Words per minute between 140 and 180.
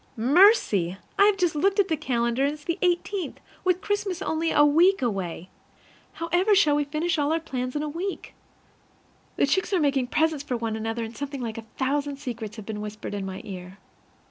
No: average, 195 wpm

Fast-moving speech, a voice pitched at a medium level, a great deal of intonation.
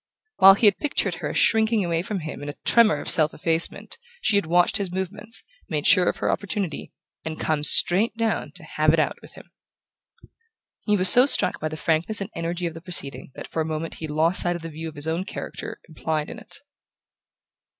No: fast, 220 wpm; medium, 175 Hz; average, 4.2 semitones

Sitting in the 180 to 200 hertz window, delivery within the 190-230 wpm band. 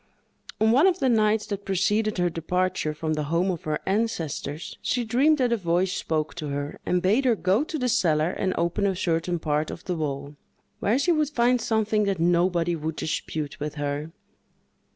Yes: medium, 185 Hz; average, 195 wpm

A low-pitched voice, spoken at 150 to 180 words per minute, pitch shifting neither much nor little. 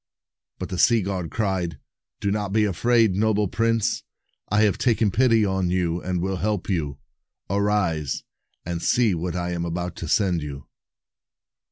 Yes: very low, 95 Hz; average, 160 wpm; average, 3.5 semitones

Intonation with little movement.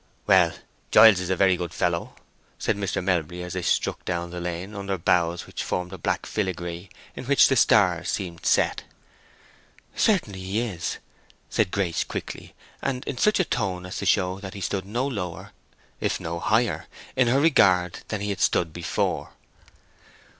No: average, 3.2 semitones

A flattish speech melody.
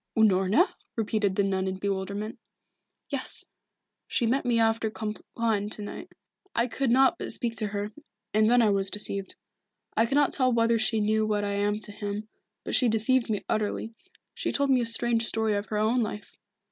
Yes: narrow, 2.1 semitones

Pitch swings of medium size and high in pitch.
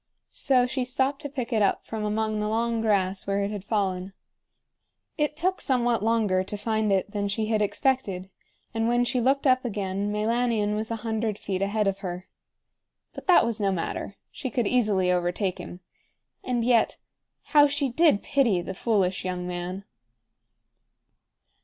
Yes: average, 3.7 semitones; high, 215 Hz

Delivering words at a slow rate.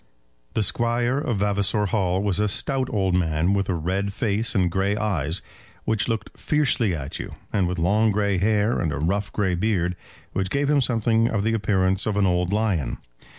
No: average, 195 wpm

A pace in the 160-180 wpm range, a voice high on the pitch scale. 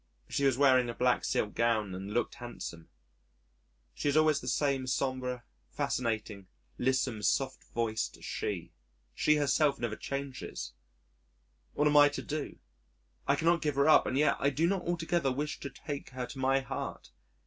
No: average, 165 wpm; low, 135 Hz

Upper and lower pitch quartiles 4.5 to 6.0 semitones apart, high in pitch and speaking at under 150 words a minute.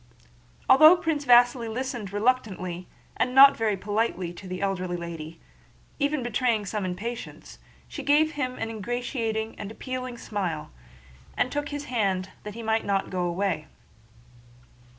Yes: average, 5.1 semitones; high, 220 Hz; average, 140 wpm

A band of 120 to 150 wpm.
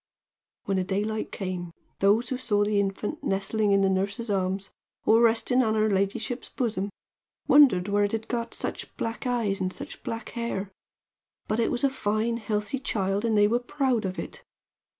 No: average, 175 wpm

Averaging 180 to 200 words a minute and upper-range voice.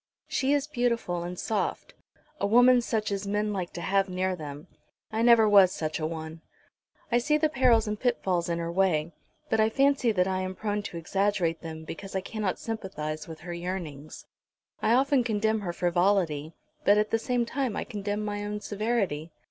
Yes: average, 190 wpm; high, 200 Hz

